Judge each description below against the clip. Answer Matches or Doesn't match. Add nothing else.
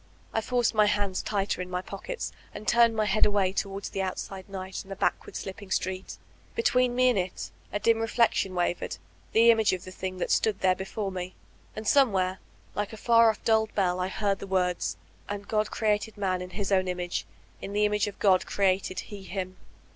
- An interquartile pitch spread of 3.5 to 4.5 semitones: Doesn't match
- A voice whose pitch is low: Doesn't match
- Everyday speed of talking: Doesn't match